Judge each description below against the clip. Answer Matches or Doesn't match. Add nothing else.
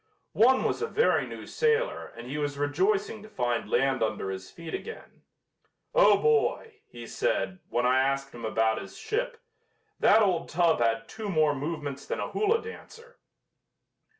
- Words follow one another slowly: Doesn't match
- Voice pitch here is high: Doesn't match